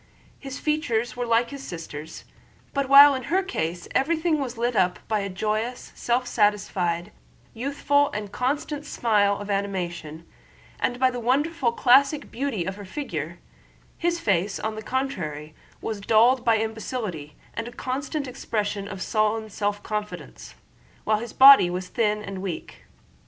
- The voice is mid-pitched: No, high, 225 Hz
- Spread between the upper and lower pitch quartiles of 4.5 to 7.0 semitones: Yes, average, 5.0 semitones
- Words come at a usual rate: Yes, average, 150 wpm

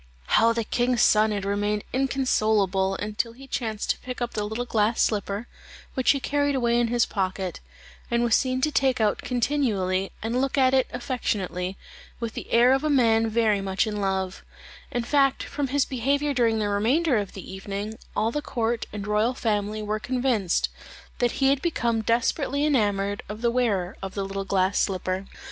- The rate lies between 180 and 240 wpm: Yes, average, 190 wpm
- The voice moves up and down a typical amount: Yes, average, 3.9 semitones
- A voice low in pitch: No, high, 225 Hz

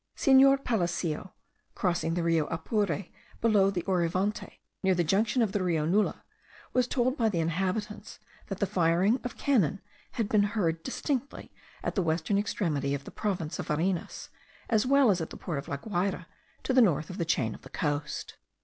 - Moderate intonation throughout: Yes, average, 4.7 semitones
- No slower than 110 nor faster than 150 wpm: No, average, 185 wpm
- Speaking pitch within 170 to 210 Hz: Yes, high, 190 Hz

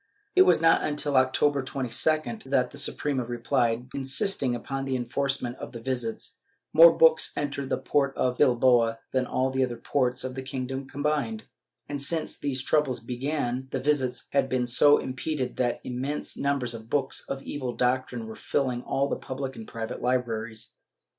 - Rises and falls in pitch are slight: Yes, narrow, 2.3 semitones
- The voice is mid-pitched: No, low, 130 Hz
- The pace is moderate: Yes, average, 170 wpm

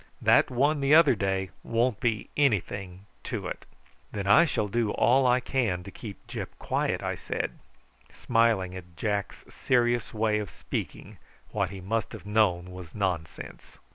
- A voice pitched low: Yes, low, 105 Hz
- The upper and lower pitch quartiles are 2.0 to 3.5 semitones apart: No, average, 4.0 semitones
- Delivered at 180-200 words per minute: No, average, 160 wpm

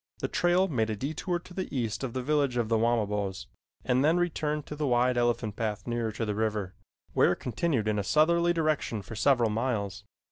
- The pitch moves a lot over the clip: Yes, wide, 5.8 semitones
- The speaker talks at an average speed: No, fast, 210 wpm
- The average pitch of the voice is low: Yes, low, 120 Hz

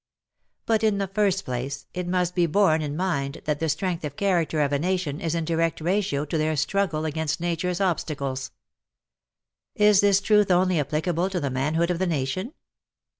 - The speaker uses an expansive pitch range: No, average, 3.8 semitones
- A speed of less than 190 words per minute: Yes, average, 180 wpm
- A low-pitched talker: No, medium, 170 Hz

